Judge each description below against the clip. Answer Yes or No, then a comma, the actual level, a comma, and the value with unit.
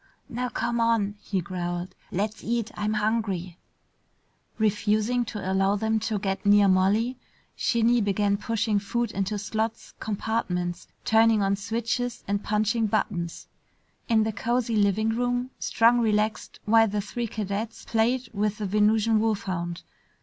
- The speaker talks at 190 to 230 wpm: No, slow, 135 wpm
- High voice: Yes, high, 215 Hz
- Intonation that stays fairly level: Yes, narrow, 2.3 semitones